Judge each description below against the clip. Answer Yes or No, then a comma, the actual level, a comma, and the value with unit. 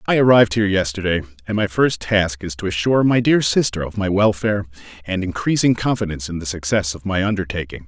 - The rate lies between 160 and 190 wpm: No, average, 200 wpm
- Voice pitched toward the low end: Yes, low, 100 Hz